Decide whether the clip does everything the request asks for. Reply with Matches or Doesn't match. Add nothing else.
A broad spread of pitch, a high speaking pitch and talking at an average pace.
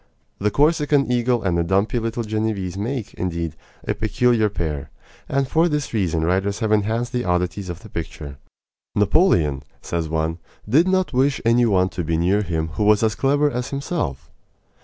Doesn't match